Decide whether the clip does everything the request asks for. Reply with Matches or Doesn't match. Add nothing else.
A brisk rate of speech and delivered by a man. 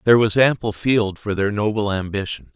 Doesn't match